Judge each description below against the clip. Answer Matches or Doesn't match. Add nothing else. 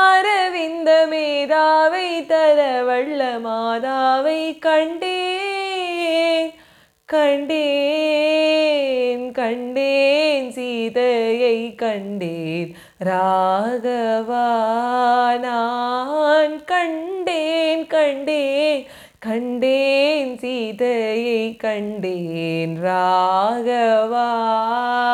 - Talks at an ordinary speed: Doesn't match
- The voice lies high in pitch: Matches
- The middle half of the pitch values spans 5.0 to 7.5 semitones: Matches